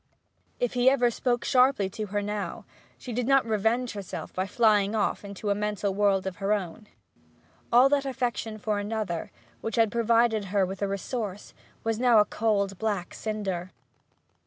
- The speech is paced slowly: No, average, 170 wpm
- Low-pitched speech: No, high, 215 Hz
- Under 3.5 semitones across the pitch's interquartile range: Yes, average, 2.9 semitones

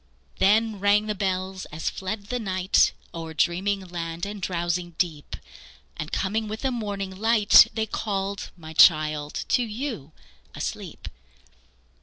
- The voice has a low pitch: No, high, 190 Hz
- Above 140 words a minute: No, slow, 135 wpm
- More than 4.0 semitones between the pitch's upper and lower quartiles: No, average, 3.6 semitones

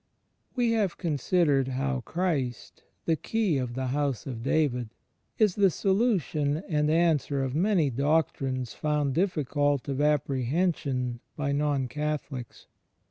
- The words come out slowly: Yes, slow, 125 wpm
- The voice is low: No, medium, 145 Hz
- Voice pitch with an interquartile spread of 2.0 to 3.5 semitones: No, average, 4.0 semitones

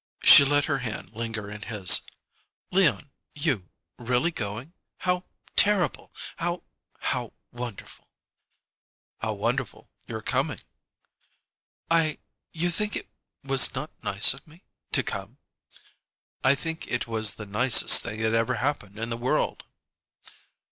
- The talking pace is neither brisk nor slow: No, slow, 125 wpm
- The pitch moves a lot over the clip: Yes, wide, 5.8 semitones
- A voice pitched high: No, low, 125 Hz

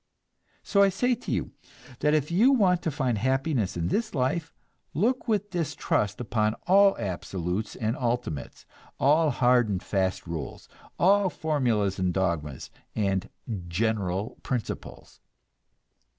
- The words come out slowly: Yes, slow, 130 wpm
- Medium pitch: No, low, 125 Hz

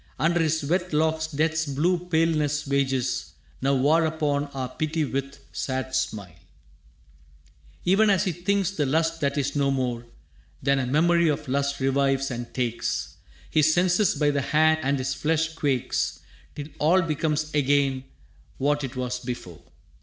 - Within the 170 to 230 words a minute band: No, average, 150 wpm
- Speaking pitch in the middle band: Yes, medium, 145 Hz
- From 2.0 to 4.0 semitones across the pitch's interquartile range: Yes, average, 3.1 semitones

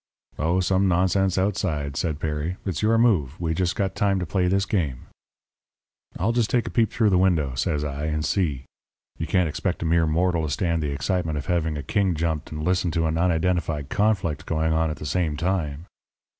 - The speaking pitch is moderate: No, very low, 85 Hz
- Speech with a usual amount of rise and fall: Yes, average, 3.4 semitones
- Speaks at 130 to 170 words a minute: No, fast, 205 wpm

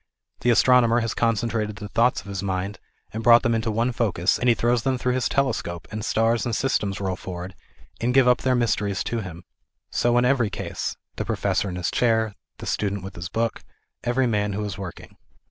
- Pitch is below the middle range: Yes, low, 115 Hz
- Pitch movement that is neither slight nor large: Yes, average, 3.4 semitones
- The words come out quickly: Yes, fast, 220 wpm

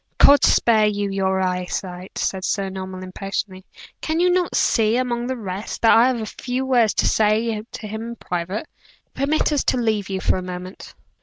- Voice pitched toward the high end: Yes, high, 215 Hz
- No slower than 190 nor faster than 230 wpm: Yes, average, 200 wpm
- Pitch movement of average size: Yes, average, 4.2 semitones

